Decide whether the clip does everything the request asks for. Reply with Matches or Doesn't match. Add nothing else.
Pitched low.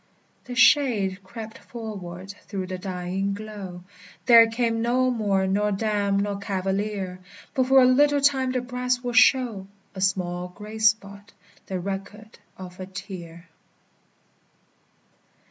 Doesn't match